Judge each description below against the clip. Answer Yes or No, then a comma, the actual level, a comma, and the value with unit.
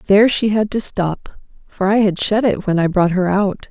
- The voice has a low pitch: No, high, 200 Hz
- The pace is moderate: No, fast, 245 wpm